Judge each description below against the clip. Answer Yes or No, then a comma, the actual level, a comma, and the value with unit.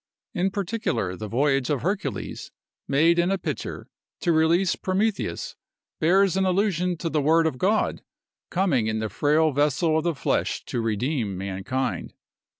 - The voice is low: No, medium, 160 Hz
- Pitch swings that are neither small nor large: No, wide, 6.0 semitones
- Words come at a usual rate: Yes, average, 150 wpm